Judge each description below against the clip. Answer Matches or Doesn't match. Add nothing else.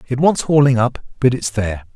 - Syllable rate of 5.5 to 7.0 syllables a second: Matches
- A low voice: Matches